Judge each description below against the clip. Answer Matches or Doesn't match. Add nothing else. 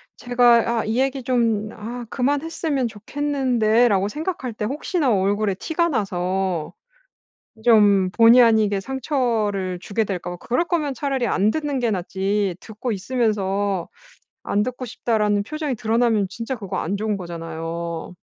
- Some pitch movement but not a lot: Matches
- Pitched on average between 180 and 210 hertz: Doesn't match